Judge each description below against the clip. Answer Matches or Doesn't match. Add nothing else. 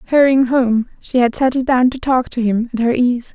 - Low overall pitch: Doesn't match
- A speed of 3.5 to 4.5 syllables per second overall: Doesn't match